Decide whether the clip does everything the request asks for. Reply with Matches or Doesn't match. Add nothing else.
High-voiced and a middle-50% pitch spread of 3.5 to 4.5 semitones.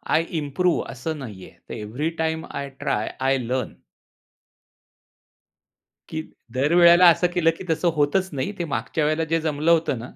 Doesn't match